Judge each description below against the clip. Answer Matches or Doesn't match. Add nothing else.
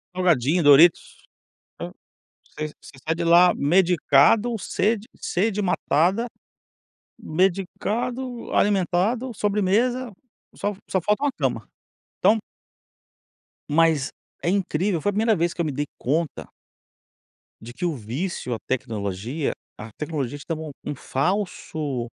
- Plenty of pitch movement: Matches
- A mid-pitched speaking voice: Matches